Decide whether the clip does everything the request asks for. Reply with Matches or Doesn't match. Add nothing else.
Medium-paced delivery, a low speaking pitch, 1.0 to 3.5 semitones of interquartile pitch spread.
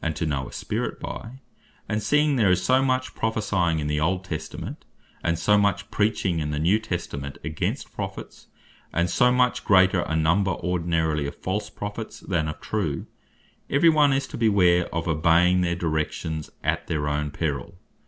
Doesn't match